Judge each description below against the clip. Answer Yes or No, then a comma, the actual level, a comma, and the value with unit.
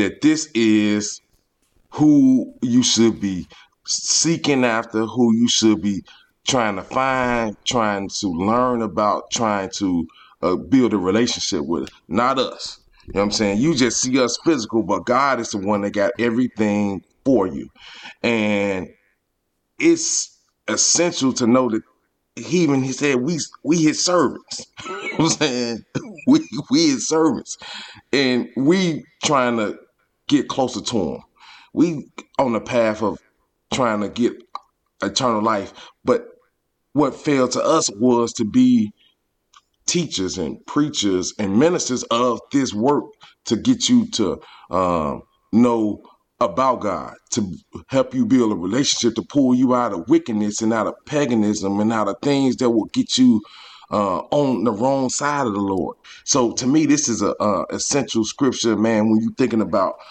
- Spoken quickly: No, average, 155 wpm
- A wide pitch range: Yes, wide, 8.5 semitones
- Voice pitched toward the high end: No, low, 125 Hz